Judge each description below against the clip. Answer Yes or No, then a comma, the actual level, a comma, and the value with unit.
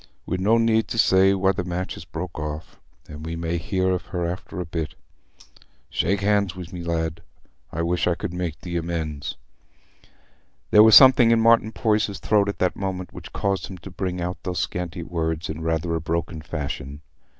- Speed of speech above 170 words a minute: Yes, average, 195 wpm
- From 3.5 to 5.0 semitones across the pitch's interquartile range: No, average, 2.9 semitones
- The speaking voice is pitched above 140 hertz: No, very low, 90 Hz